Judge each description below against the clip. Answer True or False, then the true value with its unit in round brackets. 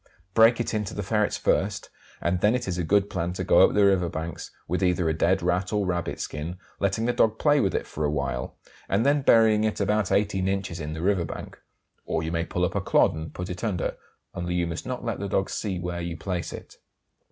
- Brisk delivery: True (245 wpm)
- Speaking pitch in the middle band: False (95 Hz)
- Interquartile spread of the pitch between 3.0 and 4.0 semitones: True (3.4 semitones)